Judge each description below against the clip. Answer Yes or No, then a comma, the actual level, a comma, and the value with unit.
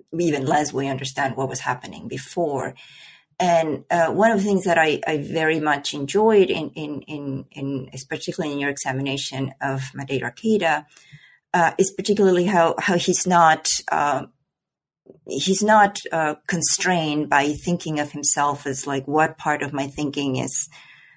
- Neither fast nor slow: Yes, average, 155 wpm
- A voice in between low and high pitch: Yes, medium, 150 Hz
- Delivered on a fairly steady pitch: No, average, 4.0 semitones